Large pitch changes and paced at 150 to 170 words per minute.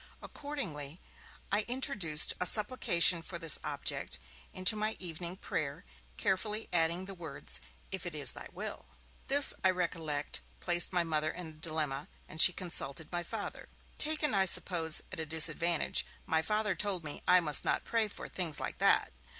No: average, 3.6 semitones; average, 165 wpm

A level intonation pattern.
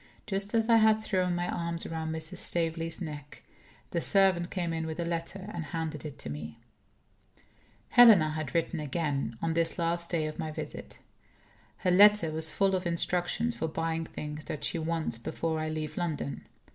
Yes: narrow, 2.3 semitones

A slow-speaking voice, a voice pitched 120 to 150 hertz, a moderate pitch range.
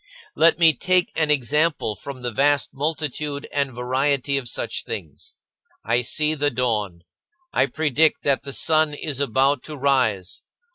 No: average, 150 wpm; medium, 140 Hz; average, 3.3 semitones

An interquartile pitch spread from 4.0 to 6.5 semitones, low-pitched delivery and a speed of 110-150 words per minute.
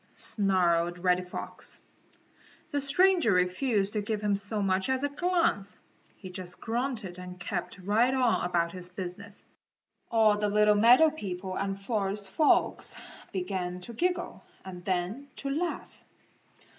No: average, 4.8 semitones; high, 200 Hz; average, 140 wpm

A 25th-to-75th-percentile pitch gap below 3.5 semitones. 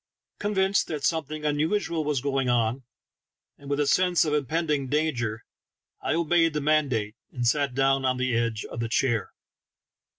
No: average, 3.9 semitones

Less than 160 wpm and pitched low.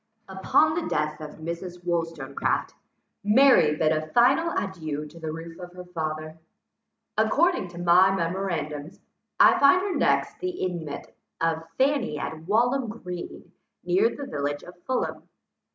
No: average, 140 wpm; medium, 175 Hz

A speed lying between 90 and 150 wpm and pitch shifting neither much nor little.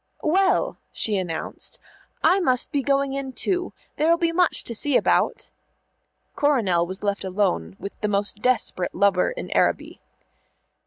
No: average, 145 wpm; wide, 7.5 semitones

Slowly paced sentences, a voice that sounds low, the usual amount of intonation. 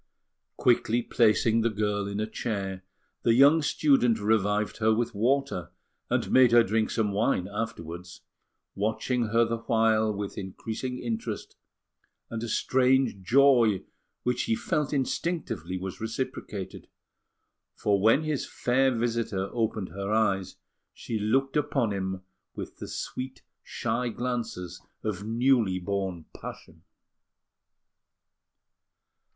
Yes: slow, 120 wpm; low, 110 Hz; average, 3.5 semitones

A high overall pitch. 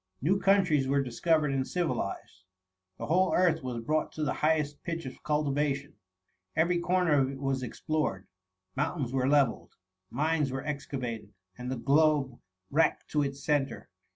No: medium, 145 Hz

